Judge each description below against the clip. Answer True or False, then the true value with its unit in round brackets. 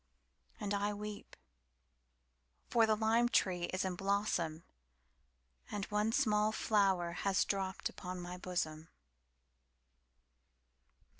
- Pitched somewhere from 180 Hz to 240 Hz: True (185 Hz)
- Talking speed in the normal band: False (90 wpm)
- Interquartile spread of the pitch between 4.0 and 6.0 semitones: True (5.0 semitones)